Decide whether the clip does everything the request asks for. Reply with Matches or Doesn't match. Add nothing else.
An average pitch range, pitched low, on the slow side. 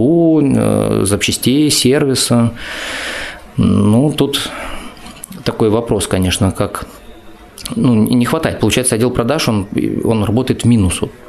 Matches